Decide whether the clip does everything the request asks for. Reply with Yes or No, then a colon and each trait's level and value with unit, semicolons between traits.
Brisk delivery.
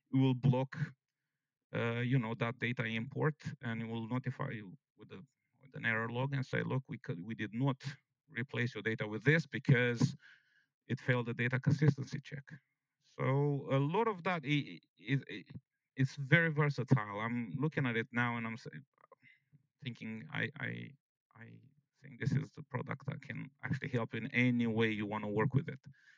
No: average, 180 wpm